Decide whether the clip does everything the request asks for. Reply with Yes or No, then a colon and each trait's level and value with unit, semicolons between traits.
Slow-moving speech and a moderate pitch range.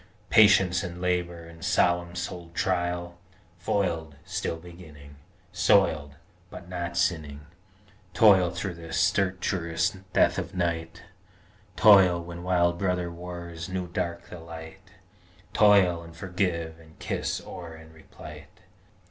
No: slow, 120 wpm; narrow, 1.6 semitones